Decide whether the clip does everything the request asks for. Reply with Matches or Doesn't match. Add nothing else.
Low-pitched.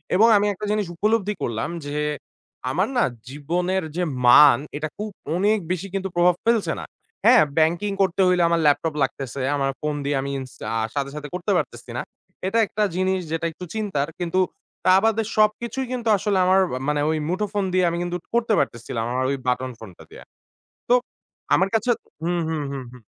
Doesn't match